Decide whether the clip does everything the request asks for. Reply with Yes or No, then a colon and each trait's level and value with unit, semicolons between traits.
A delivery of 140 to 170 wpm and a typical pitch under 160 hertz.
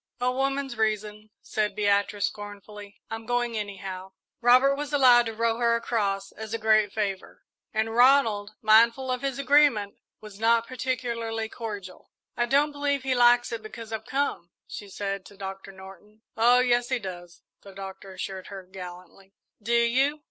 No: average, 165 wpm; high, 220 Hz